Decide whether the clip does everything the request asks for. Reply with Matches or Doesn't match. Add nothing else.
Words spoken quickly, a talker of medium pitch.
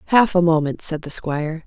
Matches